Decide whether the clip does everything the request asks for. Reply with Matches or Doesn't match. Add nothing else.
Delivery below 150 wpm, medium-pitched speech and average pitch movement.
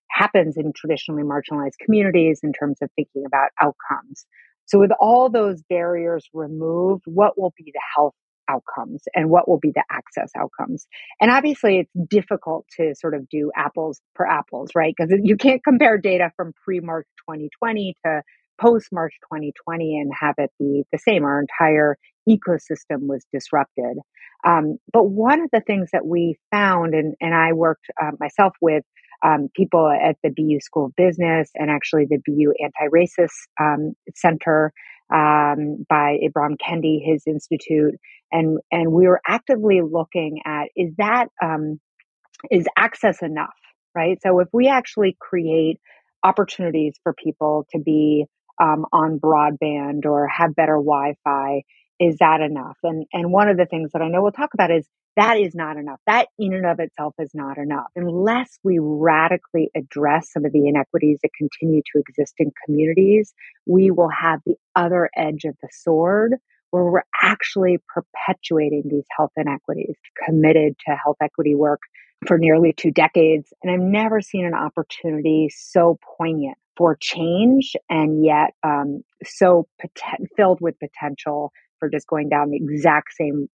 Doesn't match